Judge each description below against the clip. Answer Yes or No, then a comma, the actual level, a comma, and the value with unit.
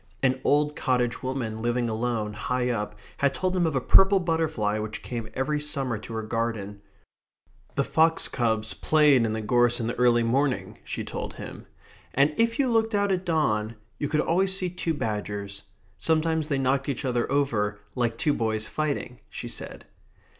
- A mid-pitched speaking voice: No, low, 130 Hz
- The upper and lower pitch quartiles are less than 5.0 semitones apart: No, wide, 5.4 semitones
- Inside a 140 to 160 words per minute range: No, average, 180 wpm